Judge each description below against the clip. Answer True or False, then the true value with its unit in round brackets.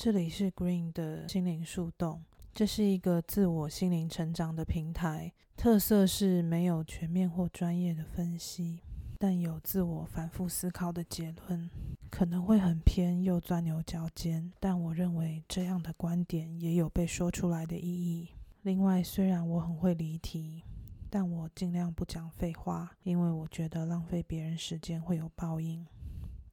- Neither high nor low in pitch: True (170 Hz)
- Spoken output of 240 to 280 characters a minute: True (250 characters per minute)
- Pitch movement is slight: True (1.6 semitones)